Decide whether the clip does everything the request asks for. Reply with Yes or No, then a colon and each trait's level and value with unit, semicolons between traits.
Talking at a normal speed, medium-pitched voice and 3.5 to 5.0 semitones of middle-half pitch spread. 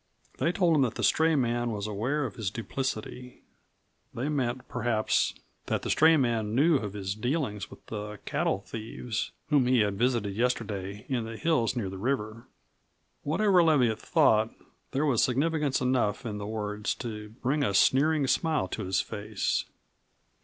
No: average, 165 wpm; low, 120 Hz; average, 4.5 semitones